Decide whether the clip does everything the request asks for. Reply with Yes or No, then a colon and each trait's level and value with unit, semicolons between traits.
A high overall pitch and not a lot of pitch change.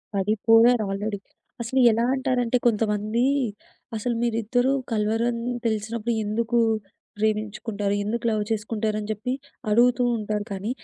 Yes: high, 220 Hz; narrow, 2.0 semitones